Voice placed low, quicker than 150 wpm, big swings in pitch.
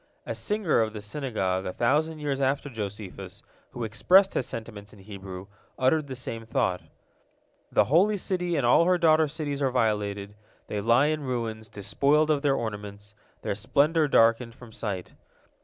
Yes: low, 120 Hz; average, 165 wpm; wide, 6.2 semitones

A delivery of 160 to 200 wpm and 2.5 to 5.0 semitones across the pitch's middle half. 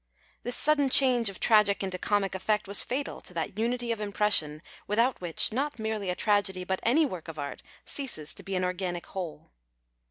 Yes: average, 190 wpm; average, 4.3 semitones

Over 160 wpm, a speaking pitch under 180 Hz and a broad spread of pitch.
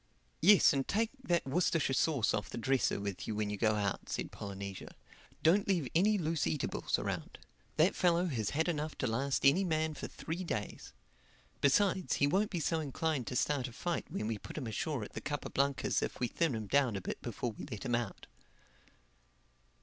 Yes: average, 200 wpm; medium, 140 Hz; wide, 6.5 semitones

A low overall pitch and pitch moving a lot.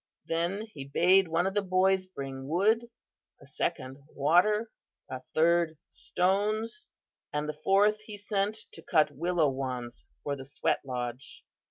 No: medium, 175 Hz; wide, 6.0 semitones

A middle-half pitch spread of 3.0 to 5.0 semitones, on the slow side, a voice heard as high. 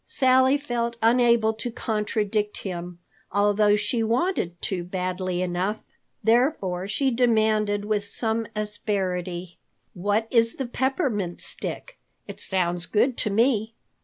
Yes: average, 3.8 semitones; slow, 120 wpm; high, 215 Hz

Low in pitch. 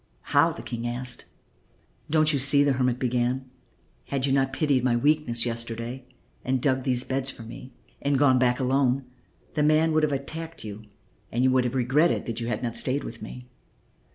Yes: low, 130 Hz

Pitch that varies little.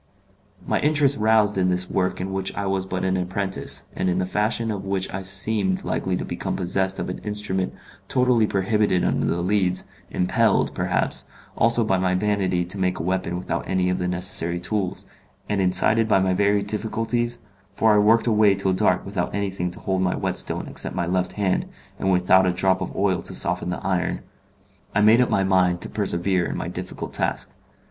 Yes: narrow, 2.3 semitones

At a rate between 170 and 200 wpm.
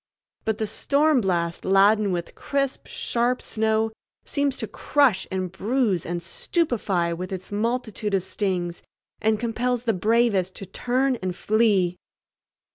No: slow, 135 wpm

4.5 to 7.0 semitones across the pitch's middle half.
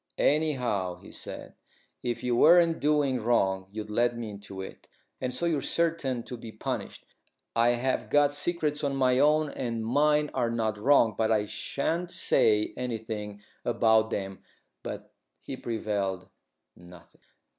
Yes: average, 5.2 semitones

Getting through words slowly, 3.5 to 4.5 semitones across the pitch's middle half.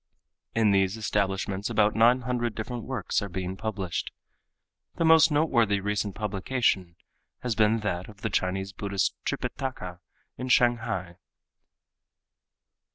Yes: slow, 120 wpm; average, 3.8 semitones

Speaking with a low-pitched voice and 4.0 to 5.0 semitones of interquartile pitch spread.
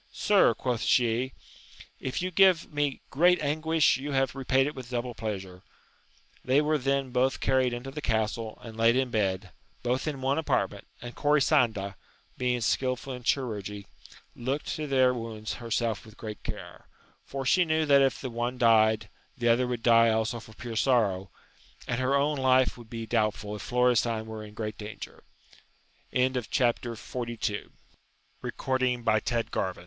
No: low, 125 Hz; average, 3.4 semitones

